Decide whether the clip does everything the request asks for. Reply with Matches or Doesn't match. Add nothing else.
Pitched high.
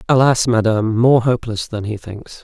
Doesn't match